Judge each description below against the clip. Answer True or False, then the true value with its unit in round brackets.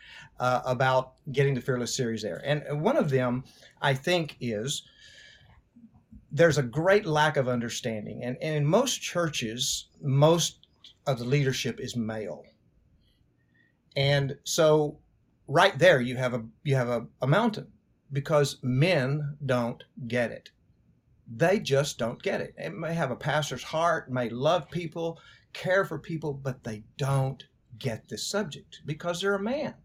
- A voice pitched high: False (140 Hz)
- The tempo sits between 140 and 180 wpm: True (150 wpm)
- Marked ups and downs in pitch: False (4.3 semitones)